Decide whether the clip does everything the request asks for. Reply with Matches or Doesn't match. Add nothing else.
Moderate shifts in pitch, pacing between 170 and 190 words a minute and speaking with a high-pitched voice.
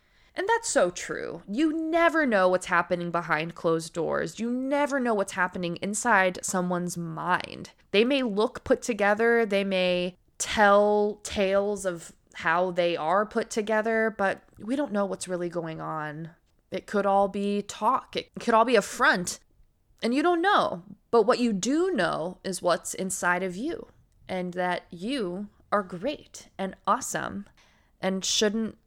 Doesn't match